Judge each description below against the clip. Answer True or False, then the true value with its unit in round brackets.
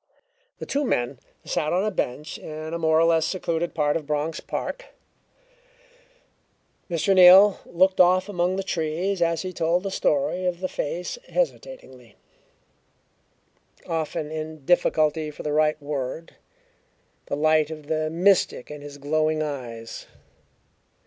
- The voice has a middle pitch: True (160 Hz)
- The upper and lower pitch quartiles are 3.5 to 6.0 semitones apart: False (3.1 semitones)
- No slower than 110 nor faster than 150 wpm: True (140 wpm)